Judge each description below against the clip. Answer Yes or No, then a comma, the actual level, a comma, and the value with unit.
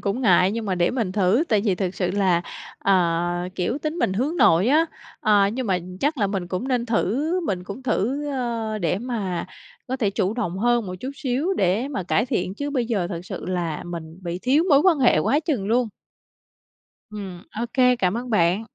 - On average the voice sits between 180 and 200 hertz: No, high, 210 Hz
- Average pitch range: No, wide, 5.7 semitones